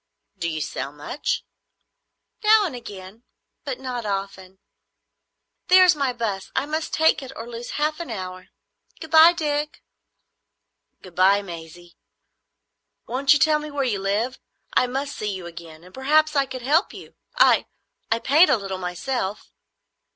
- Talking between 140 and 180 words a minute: Yes, average, 155 wpm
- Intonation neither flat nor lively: No, wide, 7.7 semitones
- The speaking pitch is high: Yes, high, 245 Hz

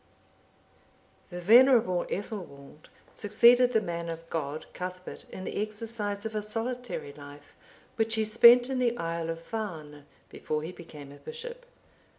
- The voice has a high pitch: Yes, high, 205 Hz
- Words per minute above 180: No, average, 150 wpm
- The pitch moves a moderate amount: No, wide, 5.9 semitones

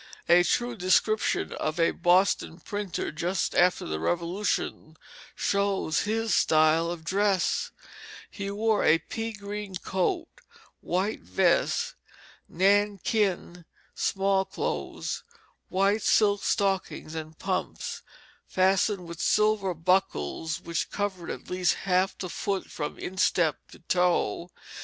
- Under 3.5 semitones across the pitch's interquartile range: Yes, average, 3.0 semitones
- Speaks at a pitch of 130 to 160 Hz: No, medium, 185 Hz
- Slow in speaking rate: Yes, slow, 115 wpm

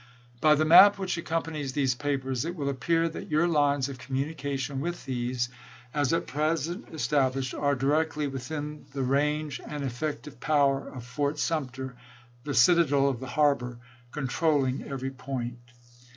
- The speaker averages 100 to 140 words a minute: No, average, 155 wpm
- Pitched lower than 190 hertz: Yes, medium, 140 Hz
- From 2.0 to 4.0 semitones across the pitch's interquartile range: Yes, average, 2.7 semitones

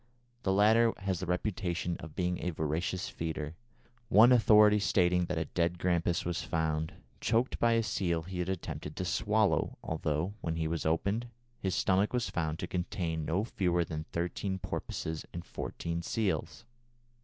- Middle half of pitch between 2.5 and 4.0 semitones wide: Yes, average, 3.4 semitones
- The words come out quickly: No, average, 165 wpm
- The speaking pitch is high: No, very low, 90 Hz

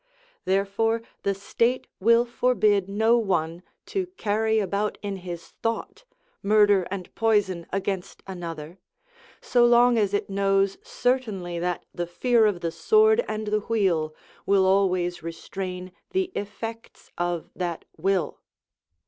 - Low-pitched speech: No, high, 200 Hz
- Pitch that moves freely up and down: No, average, 3.8 semitones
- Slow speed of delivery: Yes, slow, 130 wpm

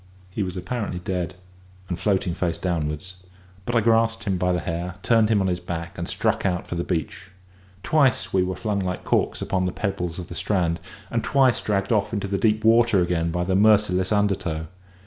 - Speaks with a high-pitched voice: No, very low, 95 Hz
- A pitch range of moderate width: Yes, average, 3.3 semitones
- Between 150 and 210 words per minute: Yes, average, 200 wpm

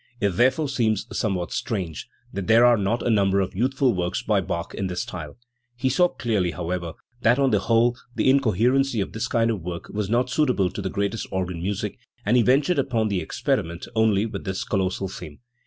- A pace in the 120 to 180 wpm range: No, fast, 205 wpm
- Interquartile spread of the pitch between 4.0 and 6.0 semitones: Yes, average, 4.5 semitones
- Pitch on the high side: No, low, 105 Hz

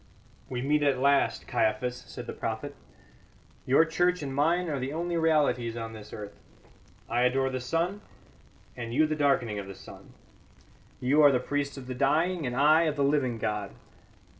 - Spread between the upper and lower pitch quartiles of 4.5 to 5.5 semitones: No, average, 3.8 semitones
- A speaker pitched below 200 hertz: Yes, medium, 140 Hz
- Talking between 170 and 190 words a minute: Yes, average, 180 wpm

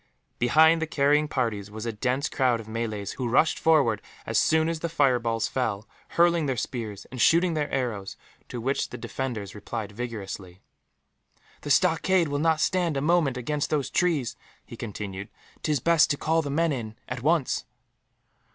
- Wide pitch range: Yes, wide, 5.7 semitones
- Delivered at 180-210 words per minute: No, average, 170 wpm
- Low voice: Yes, low, 130 Hz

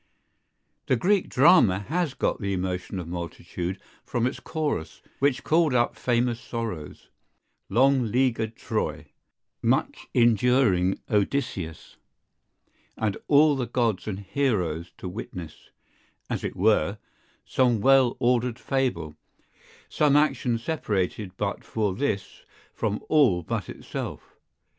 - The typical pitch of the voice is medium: No, low, 115 Hz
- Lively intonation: Yes, wide, 5.8 semitones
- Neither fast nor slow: No, slow, 115 wpm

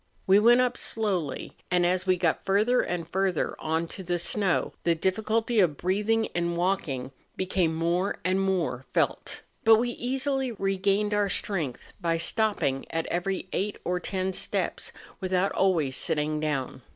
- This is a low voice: No, medium, 185 Hz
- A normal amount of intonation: Yes, average, 3.6 semitones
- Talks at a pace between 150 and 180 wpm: Yes, average, 155 wpm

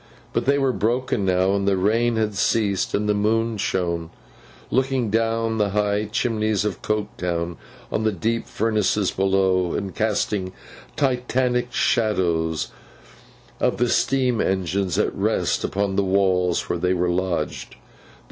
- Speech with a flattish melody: No, average, 3.4 semitones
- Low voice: Yes, low, 105 Hz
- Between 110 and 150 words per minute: Yes, average, 140 wpm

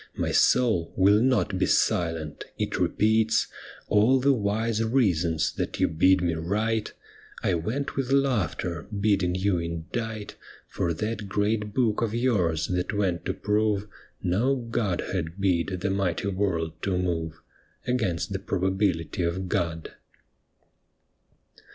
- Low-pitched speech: Yes, low, 100 Hz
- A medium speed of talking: No, slow, 130 wpm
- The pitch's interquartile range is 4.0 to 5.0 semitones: Yes, average, 4.3 semitones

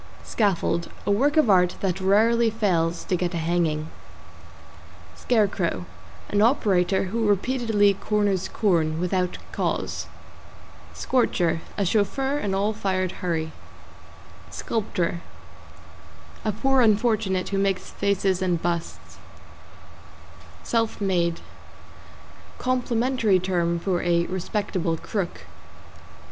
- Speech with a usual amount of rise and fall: Yes, average, 3.8 semitones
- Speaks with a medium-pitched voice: No, high, 195 Hz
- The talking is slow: Yes, slow, 105 wpm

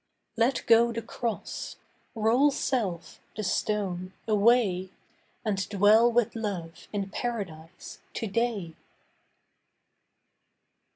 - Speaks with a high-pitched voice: Yes, high, 215 Hz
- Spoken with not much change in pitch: No, average, 3.5 semitones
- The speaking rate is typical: No, slow, 80 wpm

